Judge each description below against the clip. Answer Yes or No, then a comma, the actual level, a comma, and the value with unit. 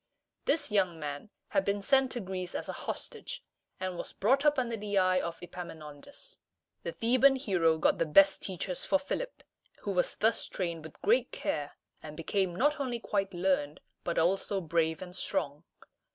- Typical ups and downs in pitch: No, wide, 6.1 semitones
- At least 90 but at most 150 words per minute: No, average, 175 wpm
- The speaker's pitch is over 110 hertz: Yes, high, 190 Hz